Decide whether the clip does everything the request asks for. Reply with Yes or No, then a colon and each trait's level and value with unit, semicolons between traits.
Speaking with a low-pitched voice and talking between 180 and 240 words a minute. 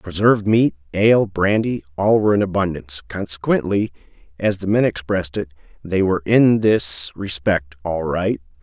No: very low, 95 Hz; average, 140 wpm